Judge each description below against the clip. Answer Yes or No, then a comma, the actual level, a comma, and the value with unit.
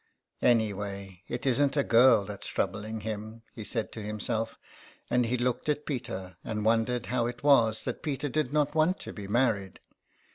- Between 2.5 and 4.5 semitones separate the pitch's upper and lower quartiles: Yes, average, 3.5 semitones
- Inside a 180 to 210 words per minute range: Yes, average, 190 wpm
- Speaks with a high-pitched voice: No, low, 115 Hz